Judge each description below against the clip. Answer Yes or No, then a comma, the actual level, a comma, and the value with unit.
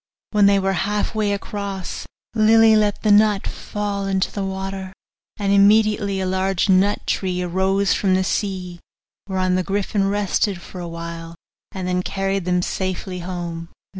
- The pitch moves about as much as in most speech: No, narrow, 1.7 semitones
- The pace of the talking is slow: No, average, 160 wpm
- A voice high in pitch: Yes, high, 195 Hz